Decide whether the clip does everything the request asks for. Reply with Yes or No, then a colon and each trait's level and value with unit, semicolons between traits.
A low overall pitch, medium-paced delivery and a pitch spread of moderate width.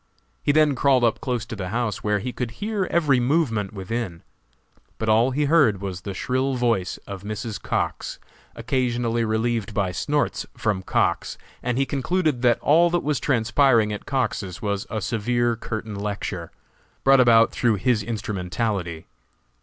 Yes: low, 115 Hz; average, 160 wpm; average, 4.0 semitones